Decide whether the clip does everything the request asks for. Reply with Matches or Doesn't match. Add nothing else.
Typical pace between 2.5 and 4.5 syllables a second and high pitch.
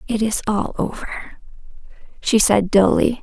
Matches